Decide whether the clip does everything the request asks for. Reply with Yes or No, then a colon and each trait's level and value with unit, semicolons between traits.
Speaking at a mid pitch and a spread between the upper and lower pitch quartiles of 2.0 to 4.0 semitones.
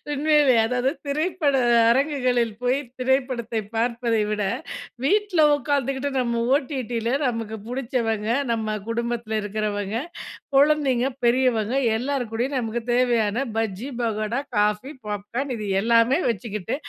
No: high, 240 Hz; average, 3.4 semitones